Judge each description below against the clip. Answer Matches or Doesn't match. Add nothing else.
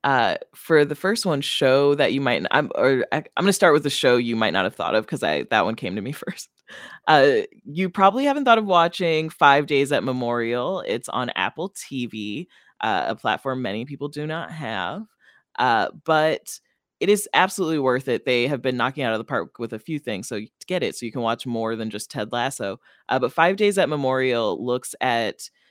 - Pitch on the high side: Doesn't match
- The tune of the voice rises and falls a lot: Matches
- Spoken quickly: Matches